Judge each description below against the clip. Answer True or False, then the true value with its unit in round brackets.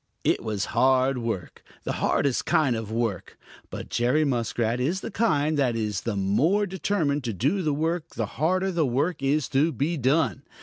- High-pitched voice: False (135 Hz)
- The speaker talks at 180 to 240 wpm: True (185 wpm)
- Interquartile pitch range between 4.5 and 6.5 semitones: True (5.5 semitones)